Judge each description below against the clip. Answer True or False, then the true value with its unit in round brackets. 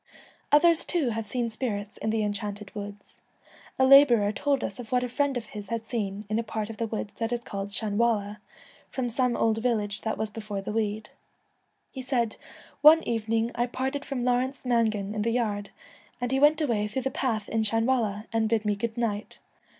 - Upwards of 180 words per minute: True (205 wpm)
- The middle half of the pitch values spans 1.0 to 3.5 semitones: True (2.9 semitones)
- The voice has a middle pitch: False (225 Hz)